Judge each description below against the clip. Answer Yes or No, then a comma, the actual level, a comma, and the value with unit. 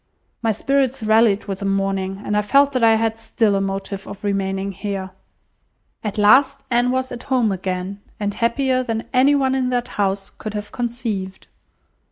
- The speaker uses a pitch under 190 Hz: No, high, 215 Hz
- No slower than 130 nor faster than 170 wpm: No, average, 180 wpm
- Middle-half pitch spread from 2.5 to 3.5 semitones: No, average, 4.1 semitones